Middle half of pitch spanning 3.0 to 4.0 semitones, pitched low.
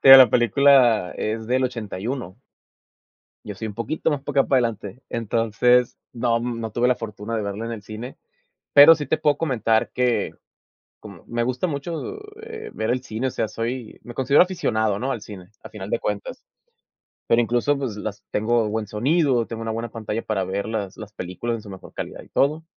Yes: average, 3.4 semitones; low, 115 Hz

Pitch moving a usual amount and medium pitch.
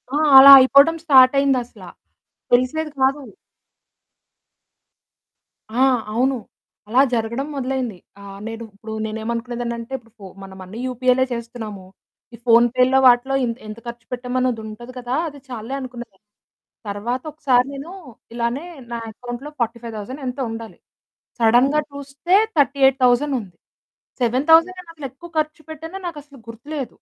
No: average, 3.0 semitones; very high, 250 Hz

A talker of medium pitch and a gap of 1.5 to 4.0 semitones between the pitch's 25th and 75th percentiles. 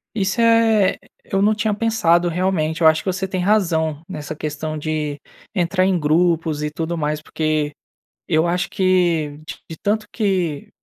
Yes: medium, 170 Hz; average, 3.7 semitones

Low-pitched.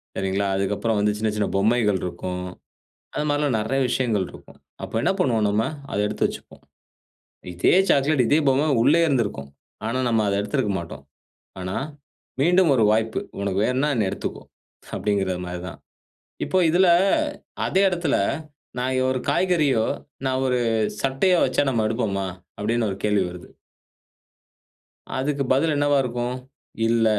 Yes: low, 115 Hz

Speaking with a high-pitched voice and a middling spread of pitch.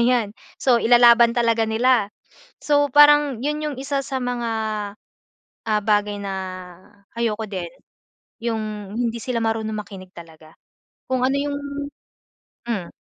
Yes: high, 235 Hz; average, 3.4 semitones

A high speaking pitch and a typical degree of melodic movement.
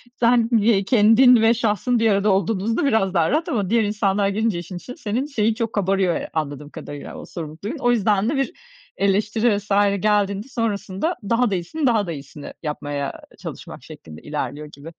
Yes: high, 205 Hz; average, 4.5 semitones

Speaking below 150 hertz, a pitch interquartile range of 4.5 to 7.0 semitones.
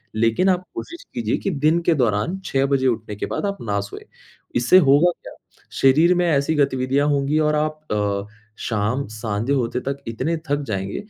Yes: low, 135 Hz; average, 5.2 semitones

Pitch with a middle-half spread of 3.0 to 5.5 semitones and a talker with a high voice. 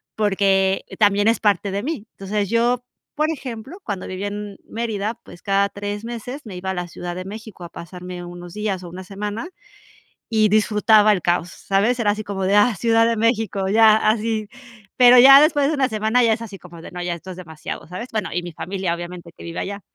Yes: average, 3.4 semitones; high, 205 Hz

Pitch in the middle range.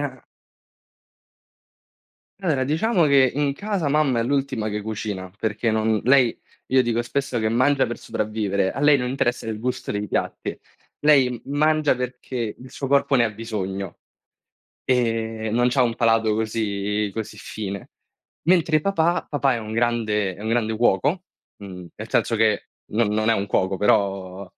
No: low, 115 Hz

